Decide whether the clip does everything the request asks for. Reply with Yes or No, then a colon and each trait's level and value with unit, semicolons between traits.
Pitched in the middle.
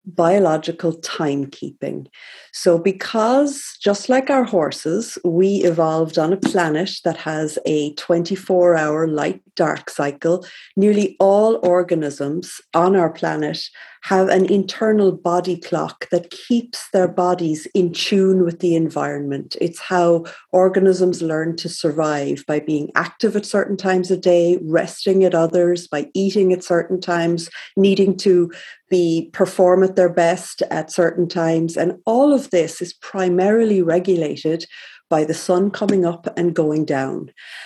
Yes: medium, 175 Hz